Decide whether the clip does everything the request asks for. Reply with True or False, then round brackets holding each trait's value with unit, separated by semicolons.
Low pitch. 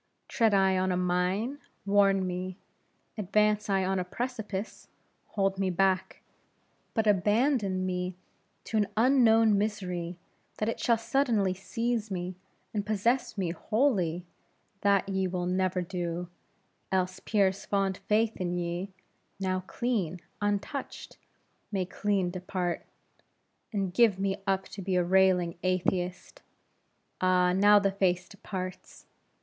False (190 Hz)